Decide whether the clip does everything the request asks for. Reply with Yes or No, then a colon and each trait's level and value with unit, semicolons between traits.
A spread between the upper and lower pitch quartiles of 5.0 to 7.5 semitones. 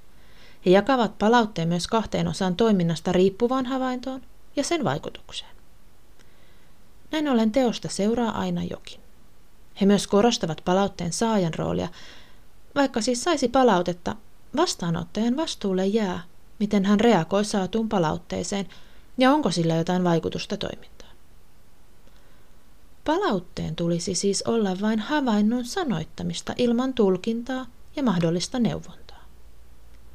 Yes: average, 5.3 semitones